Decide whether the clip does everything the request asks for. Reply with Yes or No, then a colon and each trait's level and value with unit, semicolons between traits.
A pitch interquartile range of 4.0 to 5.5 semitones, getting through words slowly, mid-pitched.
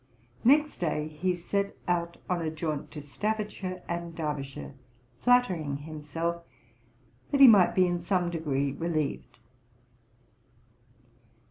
No: average, 3.4 semitones; slow, 115 wpm; medium, 170 Hz